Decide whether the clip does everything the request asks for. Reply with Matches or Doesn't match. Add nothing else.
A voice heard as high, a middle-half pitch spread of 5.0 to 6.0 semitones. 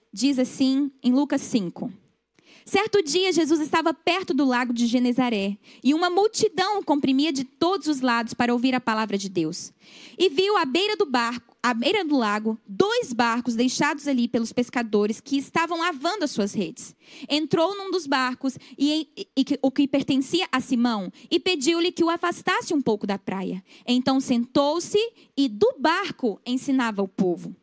Matches